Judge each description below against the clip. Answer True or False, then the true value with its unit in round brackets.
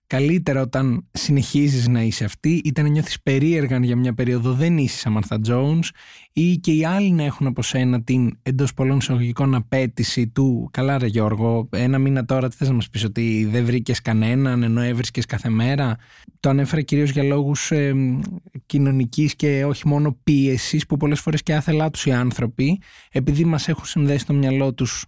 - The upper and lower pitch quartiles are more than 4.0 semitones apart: False (3.3 semitones)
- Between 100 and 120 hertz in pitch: False (135 Hz)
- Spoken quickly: True (185 wpm)